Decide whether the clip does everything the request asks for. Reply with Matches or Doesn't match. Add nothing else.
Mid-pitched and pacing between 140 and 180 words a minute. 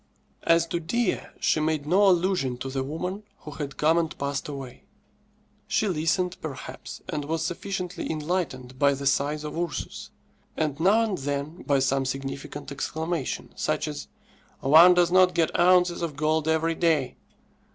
Matches